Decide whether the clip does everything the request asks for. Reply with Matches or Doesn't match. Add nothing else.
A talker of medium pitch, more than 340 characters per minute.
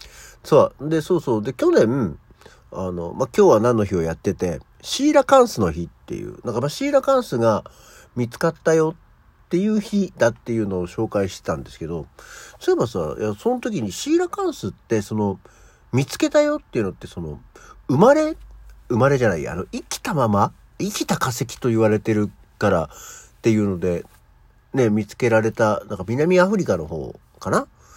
Doesn't match